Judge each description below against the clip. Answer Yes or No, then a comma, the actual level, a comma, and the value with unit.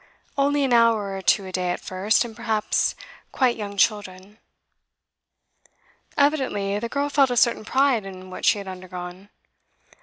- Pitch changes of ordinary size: Yes, average, 4.4 semitones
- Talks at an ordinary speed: Yes, average, 155 wpm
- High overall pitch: Yes, high, 210 Hz